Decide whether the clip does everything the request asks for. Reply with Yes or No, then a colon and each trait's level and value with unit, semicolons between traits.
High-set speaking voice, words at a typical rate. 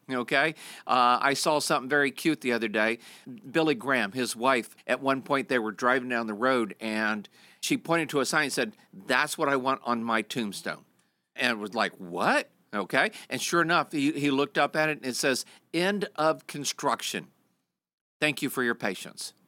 No: low, 135 Hz; average, 195 wpm